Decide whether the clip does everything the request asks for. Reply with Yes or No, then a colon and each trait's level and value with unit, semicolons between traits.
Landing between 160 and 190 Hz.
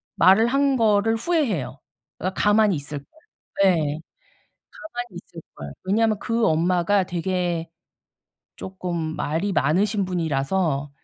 Yes: medium, 185 Hz